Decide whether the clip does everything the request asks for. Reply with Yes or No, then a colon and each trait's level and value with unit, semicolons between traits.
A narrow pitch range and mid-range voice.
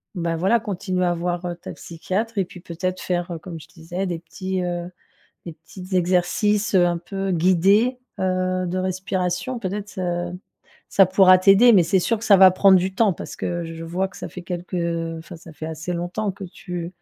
Yes: narrow, 1.8 semitones; medium, 180 Hz